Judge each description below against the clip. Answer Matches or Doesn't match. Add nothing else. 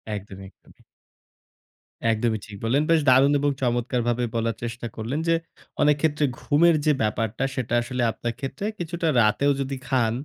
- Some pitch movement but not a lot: Matches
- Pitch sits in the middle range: Doesn't match